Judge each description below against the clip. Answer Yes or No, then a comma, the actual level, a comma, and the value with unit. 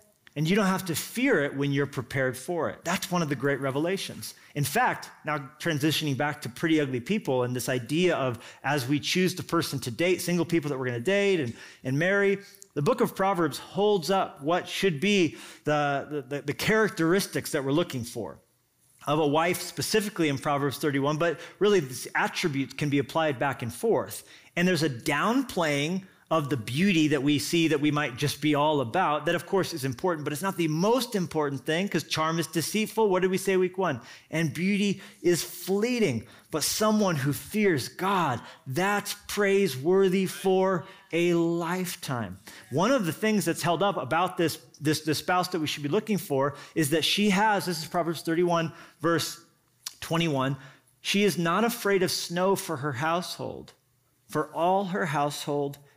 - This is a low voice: No, medium, 165 Hz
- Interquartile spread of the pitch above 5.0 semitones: No, average, 4.6 semitones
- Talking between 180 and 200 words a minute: Yes, average, 190 wpm